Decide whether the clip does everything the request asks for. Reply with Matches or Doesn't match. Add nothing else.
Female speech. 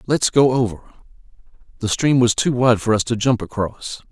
Doesn't match